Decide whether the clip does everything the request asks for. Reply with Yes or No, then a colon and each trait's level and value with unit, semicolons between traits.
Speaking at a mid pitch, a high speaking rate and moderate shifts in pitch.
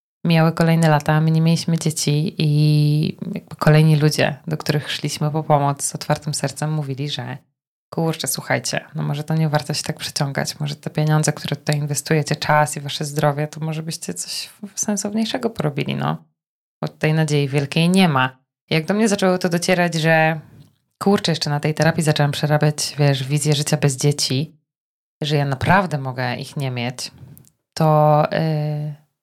No: medium, 150 Hz; fast, 170 wpm; narrow, 1.8 semitones